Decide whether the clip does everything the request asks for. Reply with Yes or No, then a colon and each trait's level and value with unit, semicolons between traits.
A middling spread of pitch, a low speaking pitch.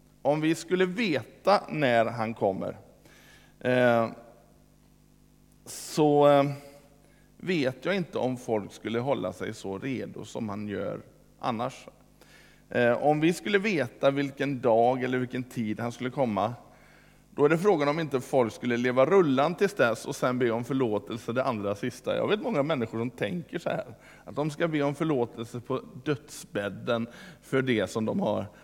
Yes: average, 3.8 semitones; low, 130 Hz